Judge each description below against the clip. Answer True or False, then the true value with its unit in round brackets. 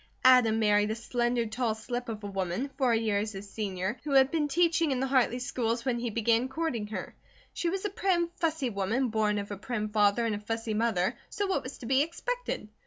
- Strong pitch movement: False (4.0 semitones)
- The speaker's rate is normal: False (220 wpm)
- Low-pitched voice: False (235 Hz)